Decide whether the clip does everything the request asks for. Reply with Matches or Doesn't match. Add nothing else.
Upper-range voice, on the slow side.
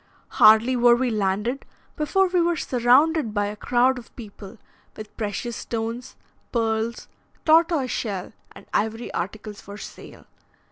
Matches